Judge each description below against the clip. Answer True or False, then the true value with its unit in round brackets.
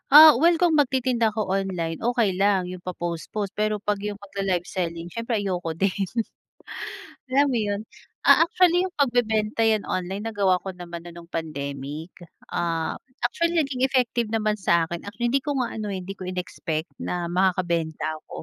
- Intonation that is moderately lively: False (5.7 semitones)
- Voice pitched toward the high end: True (200 Hz)